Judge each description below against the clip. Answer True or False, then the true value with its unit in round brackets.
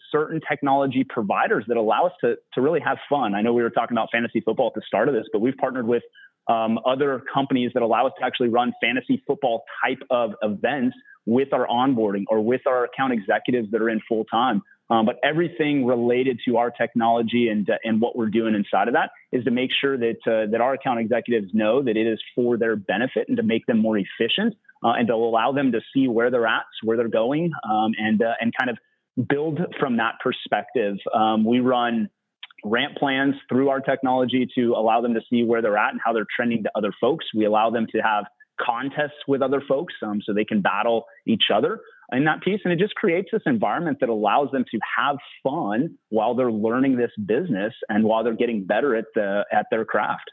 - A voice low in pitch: True (120 Hz)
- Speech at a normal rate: False (220 wpm)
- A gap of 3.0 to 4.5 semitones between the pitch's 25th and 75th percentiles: True (3.4 semitones)